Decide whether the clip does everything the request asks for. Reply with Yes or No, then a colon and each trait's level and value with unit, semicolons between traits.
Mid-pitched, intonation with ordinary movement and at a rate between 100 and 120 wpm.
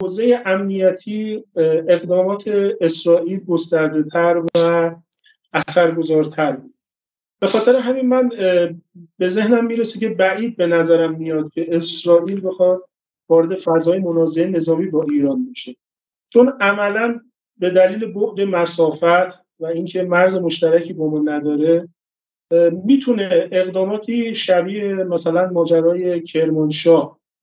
Yes: medium, 175 Hz; average, 3.2 semitones; average, 110 wpm